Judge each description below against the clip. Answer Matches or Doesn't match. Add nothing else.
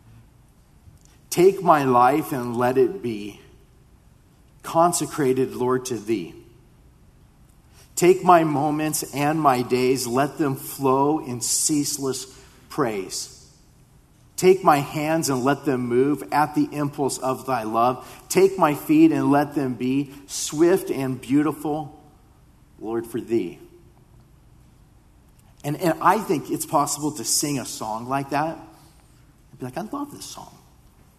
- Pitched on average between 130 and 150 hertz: Matches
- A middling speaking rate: Doesn't match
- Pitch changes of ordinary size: Matches